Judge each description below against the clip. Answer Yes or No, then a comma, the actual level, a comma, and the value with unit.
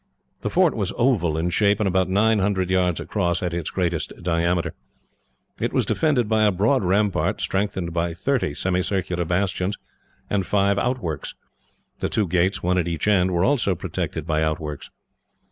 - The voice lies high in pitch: No, very low, 95 Hz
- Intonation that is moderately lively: Yes, average, 3.1 semitones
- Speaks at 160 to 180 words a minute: Yes, average, 165 wpm